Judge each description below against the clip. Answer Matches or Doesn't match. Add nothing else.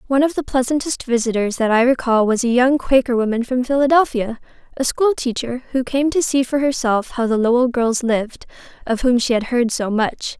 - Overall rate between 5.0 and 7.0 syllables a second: Matches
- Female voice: Matches